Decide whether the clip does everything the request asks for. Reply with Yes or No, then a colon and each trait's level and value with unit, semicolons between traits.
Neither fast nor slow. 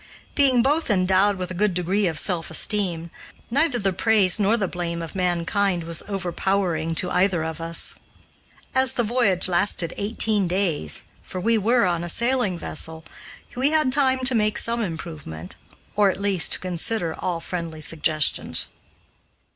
Yes: average, 160 wpm